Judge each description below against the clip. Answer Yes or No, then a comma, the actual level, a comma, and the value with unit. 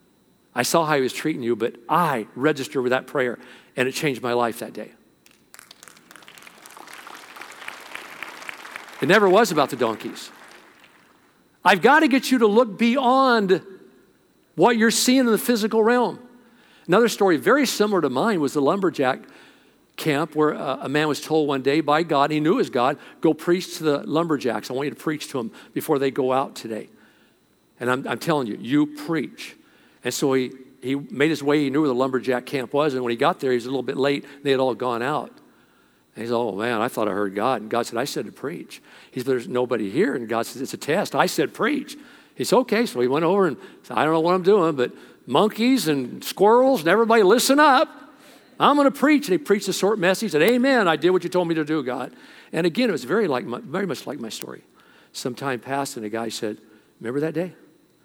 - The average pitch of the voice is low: No, medium, 150 Hz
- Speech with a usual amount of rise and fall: No, wide, 9.0 semitones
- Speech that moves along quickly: Yes, fast, 225 wpm